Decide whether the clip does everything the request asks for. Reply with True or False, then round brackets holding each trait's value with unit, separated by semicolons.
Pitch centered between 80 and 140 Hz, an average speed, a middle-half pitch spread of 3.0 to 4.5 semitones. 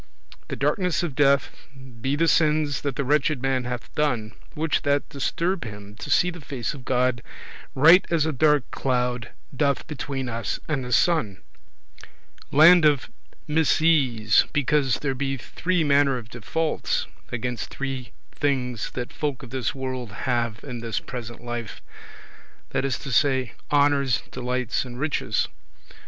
True (135 Hz; 150 wpm; 3.4 semitones)